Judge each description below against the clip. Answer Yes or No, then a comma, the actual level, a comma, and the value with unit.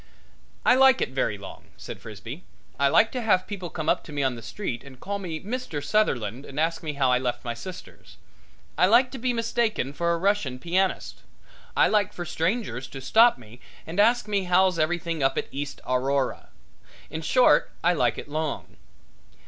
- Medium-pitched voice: Yes, medium, 165 Hz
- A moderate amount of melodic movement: No, wide, 7.3 semitones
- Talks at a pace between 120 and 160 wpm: No, average, 195 wpm